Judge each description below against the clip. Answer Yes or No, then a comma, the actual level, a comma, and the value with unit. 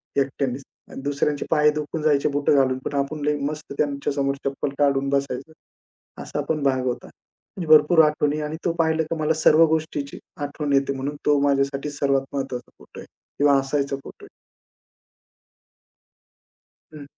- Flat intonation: Yes, narrow, 1.6 semitones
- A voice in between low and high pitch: Yes, medium, 145 Hz